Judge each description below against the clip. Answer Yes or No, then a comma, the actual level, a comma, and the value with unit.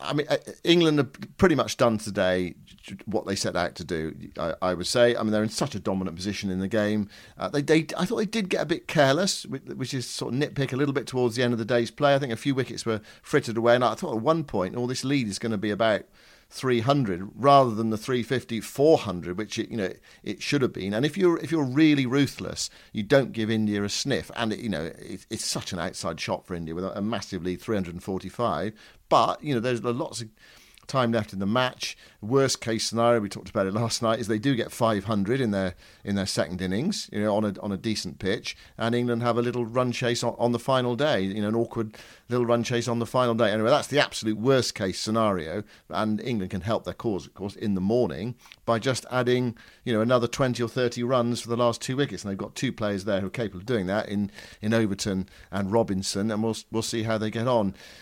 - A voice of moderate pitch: No, low, 115 Hz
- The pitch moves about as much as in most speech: Yes, average, 3.9 semitones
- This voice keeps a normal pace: No, fast, 250 wpm